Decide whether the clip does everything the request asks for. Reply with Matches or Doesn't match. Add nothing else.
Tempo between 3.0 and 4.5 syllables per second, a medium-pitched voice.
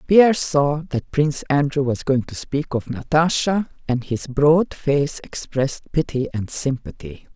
Matches